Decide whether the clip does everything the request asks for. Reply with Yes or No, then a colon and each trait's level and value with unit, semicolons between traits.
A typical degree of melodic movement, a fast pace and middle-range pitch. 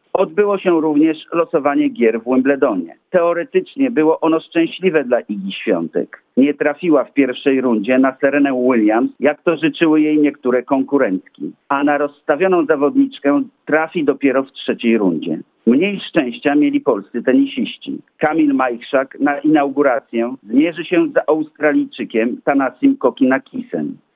No: average, 4.1 semitones; average, 130 wpm; medium, 145 Hz